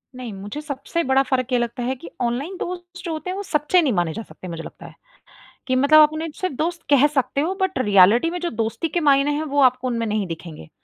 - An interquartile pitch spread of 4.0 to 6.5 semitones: Yes, wide, 5.4 semitones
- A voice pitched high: Yes, very high, 275 Hz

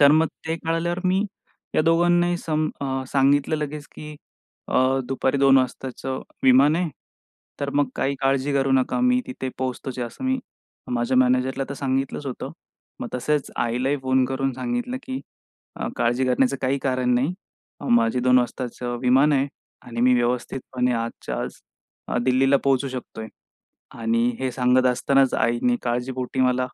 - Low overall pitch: Yes, low, 130 Hz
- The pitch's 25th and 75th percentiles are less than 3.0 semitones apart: Yes, narrow, 2.5 semitones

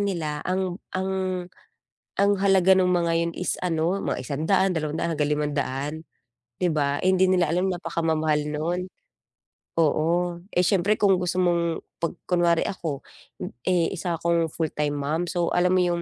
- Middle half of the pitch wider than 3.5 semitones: No, narrow, 2.6 semitones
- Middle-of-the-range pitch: Yes, medium, 170 Hz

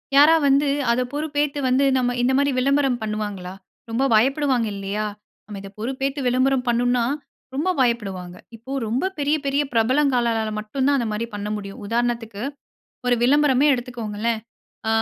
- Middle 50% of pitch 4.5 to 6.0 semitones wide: No, average, 3.9 semitones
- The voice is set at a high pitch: Yes, high, 245 Hz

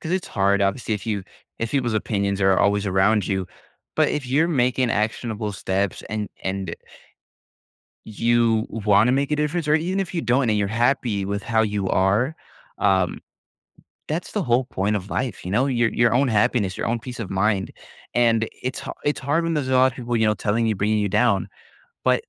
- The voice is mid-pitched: No, low, 110 Hz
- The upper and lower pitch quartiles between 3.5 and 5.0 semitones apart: Yes, average, 4.1 semitones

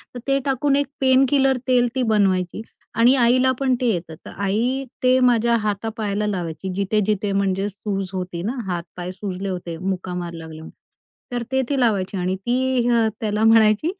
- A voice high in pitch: Yes, high, 210 Hz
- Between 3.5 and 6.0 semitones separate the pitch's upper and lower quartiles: Yes, average, 5.1 semitones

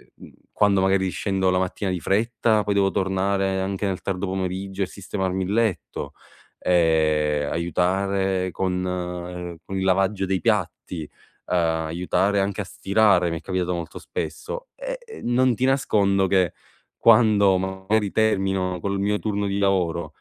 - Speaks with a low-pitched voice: Yes, very low, 95 Hz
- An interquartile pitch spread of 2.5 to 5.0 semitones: No, narrow, 1.8 semitones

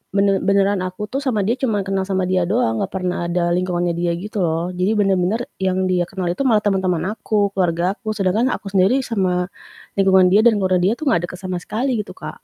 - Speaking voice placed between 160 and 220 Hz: Yes, high, 190 Hz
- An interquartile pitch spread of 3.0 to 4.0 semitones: No, narrow, 2.6 semitones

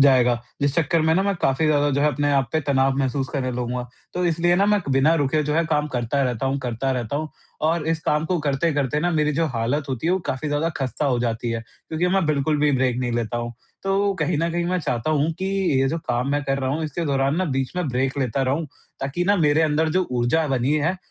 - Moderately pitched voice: Yes, medium, 145 Hz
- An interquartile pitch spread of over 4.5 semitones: No, average, 3.6 semitones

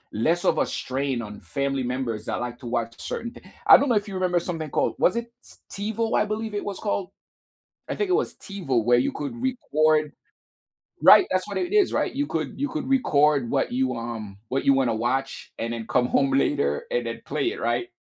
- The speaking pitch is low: No, medium, 150 Hz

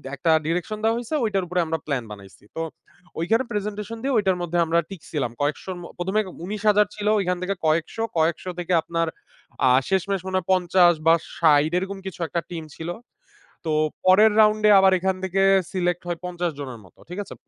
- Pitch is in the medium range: Yes, medium, 180 Hz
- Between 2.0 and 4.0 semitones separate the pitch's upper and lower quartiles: Yes, average, 3.4 semitones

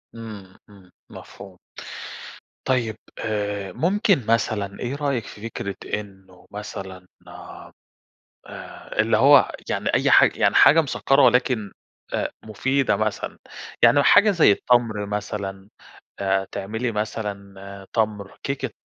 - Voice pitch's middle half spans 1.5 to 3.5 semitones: No, average, 4.0 semitones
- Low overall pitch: Yes, low, 105 Hz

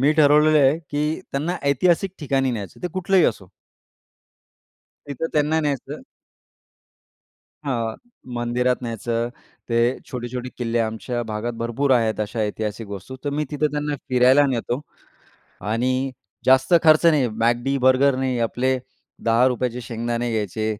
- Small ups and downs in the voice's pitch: No, average, 3.8 semitones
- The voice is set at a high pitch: No, low, 125 Hz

